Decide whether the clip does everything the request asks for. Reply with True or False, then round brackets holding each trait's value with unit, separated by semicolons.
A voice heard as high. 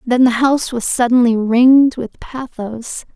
True (250 Hz)